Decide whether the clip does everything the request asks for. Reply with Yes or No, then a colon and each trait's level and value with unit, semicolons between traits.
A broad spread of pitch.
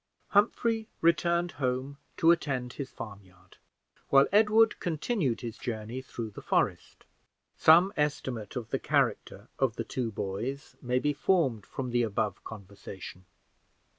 Yes: wide, 6.8 semitones